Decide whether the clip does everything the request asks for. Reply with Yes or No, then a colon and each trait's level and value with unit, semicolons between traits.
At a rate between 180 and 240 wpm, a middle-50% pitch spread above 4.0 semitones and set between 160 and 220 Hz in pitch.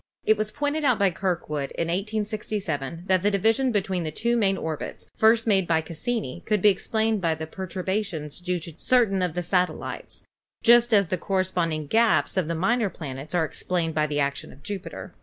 Yes: average, 195 wpm; average, 4.8 semitones; medium, 185 Hz